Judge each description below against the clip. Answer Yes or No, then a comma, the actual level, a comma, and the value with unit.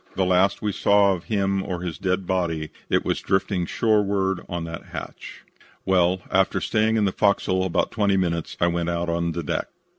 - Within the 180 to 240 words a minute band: Yes, average, 185 wpm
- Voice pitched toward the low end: Yes, very low, 95 Hz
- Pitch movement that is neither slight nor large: No, narrow, 2.3 semitones